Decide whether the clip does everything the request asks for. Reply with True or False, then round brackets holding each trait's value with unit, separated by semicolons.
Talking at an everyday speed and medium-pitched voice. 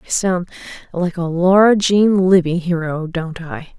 True (160 wpm; 175 Hz)